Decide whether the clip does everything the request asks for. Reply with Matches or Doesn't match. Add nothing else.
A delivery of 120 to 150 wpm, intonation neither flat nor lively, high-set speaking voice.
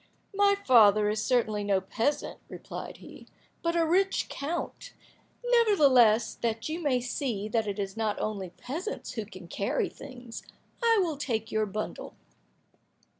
Doesn't match